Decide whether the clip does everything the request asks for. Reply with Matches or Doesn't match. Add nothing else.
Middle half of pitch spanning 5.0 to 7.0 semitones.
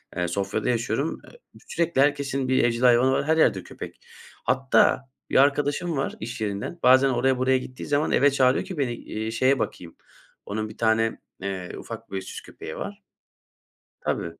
Doesn't match